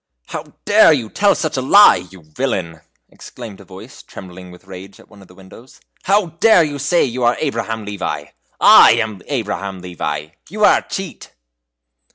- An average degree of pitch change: No, wide, 7.7 semitones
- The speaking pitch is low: Yes, low, 110 Hz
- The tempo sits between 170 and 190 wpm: Yes, average, 180 wpm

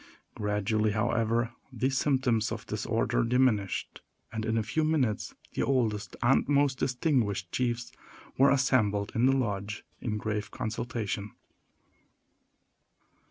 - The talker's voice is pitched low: Yes, low, 115 Hz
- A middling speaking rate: No, slow, 115 wpm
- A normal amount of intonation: Yes, average, 3.5 semitones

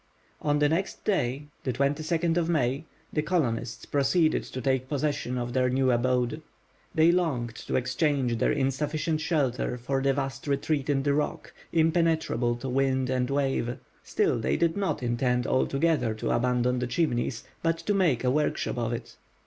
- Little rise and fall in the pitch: No, average, 3.8 semitones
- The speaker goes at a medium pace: Yes, average, 160 wpm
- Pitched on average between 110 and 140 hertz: Yes, low, 135 Hz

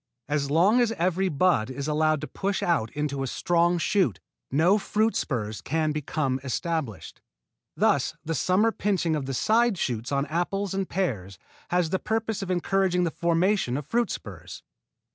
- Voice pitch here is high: No, medium, 170 Hz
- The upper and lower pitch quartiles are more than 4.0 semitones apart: Yes, wide, 5.5 semitones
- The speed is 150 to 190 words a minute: Yes, average, 165 wpm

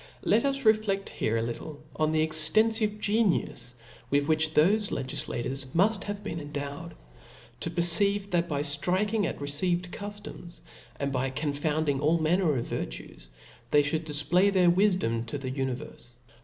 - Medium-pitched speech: Yes, medium, 160 Hz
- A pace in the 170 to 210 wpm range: No, average, 150 wpm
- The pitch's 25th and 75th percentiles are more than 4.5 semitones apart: Yes, wide, 5.6 semitones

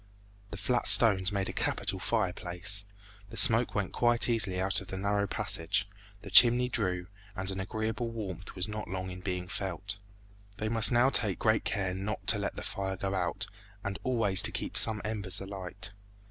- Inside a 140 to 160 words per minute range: No, average, 185 wpm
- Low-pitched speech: Yes, low, 100 Hz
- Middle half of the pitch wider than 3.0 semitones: No, narrow, 2.6 semitones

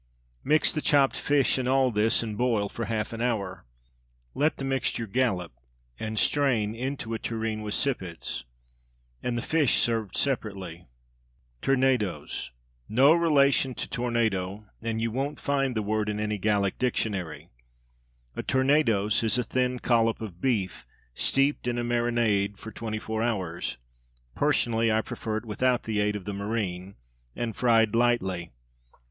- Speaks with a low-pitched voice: Yes, low, 115 Hz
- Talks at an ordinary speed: Yes, average, 150 wpm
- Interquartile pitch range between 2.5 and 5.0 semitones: Yes, average, 3.4 semitones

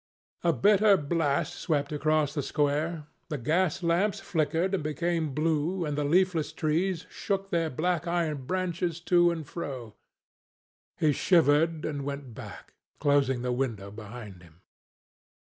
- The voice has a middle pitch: Yes, medium, 155 Hz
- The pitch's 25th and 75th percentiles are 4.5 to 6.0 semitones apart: No, average, 3.4 semitones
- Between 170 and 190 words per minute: No, average, 140 wpm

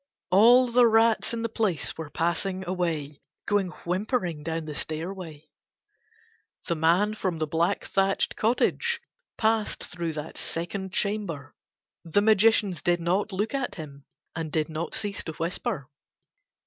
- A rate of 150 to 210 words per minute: No, average, 140 wpm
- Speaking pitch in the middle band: Yes, medium, 180 Hz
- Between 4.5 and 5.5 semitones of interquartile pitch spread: Yes, average, 4.8 semitones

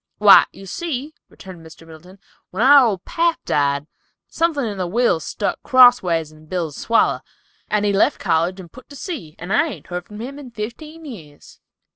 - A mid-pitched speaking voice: No, high, 205 Hz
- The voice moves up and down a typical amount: No, wide, 7.5 semitones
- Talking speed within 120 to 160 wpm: No, average, 185 wpm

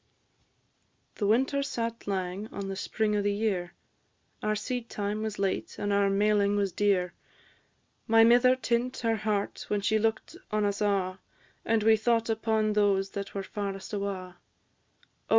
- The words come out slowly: No, average, 150 wpm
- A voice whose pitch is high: Yes, high, 210 Hz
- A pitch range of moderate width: No, narrow, 2.0 semitones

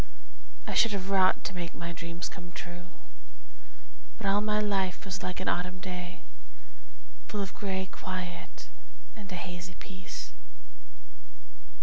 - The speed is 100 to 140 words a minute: Yes, slow, 135 wpm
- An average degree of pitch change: No, narrow, 1.9 semitones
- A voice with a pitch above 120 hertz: Yes, medium, 185 Hz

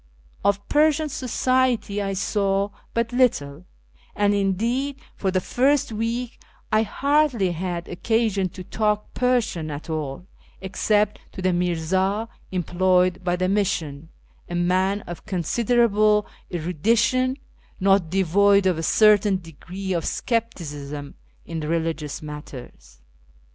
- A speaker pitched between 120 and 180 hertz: No, high, 195 Hz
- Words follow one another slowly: Yes, slow, 120 wpm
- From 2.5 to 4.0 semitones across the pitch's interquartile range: No, average, 4.4 semitones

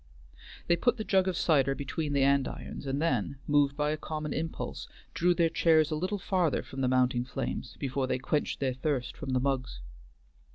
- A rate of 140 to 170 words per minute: No, average, 195 wpm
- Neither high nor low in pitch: Yes, medium, 145 Hz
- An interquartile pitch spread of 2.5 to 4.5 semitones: Yes, average, 3.4 semitones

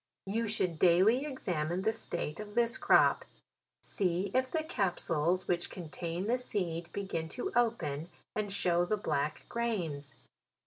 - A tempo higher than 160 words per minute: No, average, 140 wpm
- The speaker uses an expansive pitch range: No, average, 4.8 semitones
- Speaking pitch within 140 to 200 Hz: Yes, medium, 185 Hz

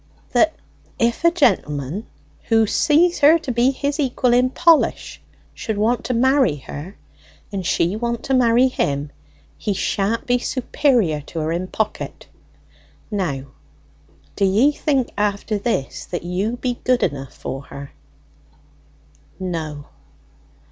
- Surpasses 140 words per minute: No, slow, 135 wpm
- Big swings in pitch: Yes, wide, 6.6 semitones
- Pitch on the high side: Yes, high, 225 Hz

